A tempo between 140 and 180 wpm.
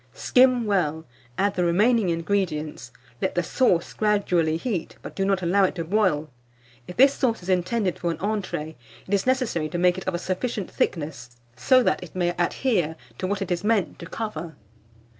No: average, 190 wpm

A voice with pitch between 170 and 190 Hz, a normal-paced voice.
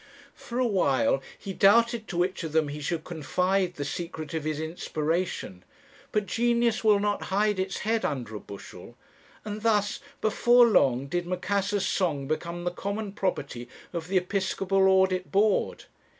Yes: medium, 185 Hz; average, 160 wpm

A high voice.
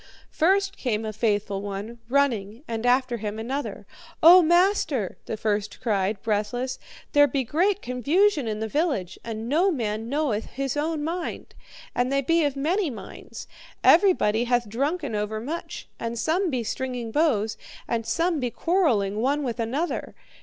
Yes: very high, 250 Hz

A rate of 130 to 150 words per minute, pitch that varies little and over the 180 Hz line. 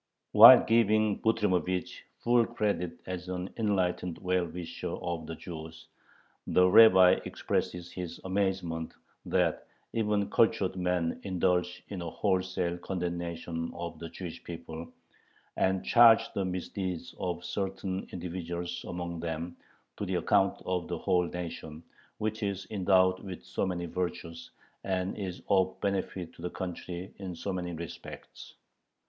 No: slow, 135 wpm; narrow, 1.9 semitones; very low, 90 Hz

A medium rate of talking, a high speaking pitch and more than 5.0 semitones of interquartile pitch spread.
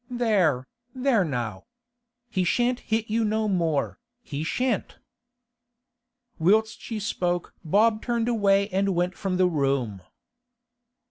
No: slow, 120 wpm; high, 195 Hz; wide, 5.4 semitones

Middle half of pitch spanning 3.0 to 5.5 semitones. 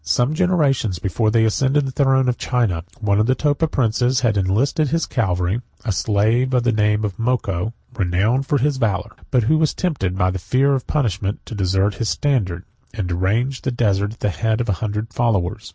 Yes: average, 4.8 semitones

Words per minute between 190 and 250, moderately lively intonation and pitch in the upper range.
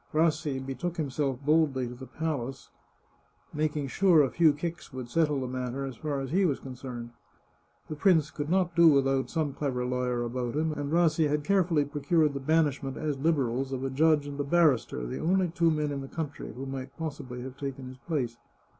No: average, 200 wpm; average, 3.3 semitones; medium, 145 Hz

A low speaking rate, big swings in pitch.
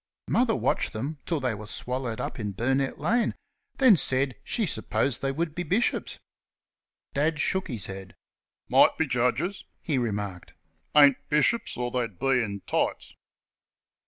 No: average, 150 wpm; wide, 5.8 semitones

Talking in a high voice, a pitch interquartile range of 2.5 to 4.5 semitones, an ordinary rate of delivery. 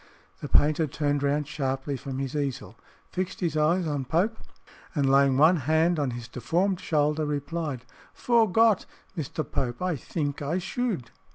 No: medium, 150 Hz; average, 3.8 semitones; average, 160 wpm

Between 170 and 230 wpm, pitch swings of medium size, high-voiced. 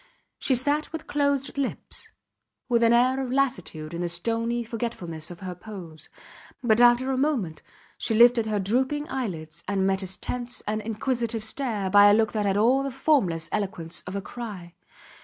Yes: average, 175 wpm; average, 5.0 semitones; high, 225 Hz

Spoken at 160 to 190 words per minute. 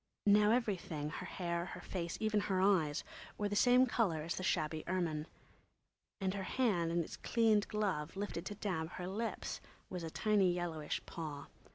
Yes: average, 175 wpm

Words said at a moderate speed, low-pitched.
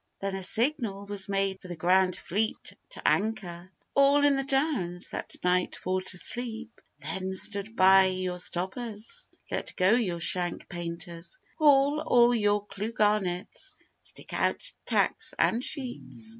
No: average, 145 wpm; high, 195 Hz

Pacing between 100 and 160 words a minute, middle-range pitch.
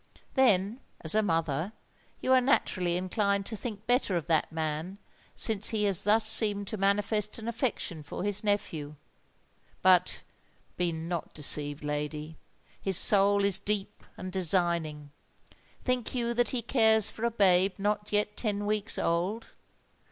No: average, 145 wpm; high, 200 Hz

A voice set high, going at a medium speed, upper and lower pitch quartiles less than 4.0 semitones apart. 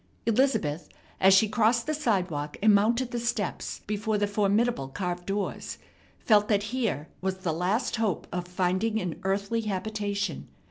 Yes: high, 205 Hz; average, 150 wpm; average, 3.2 semitones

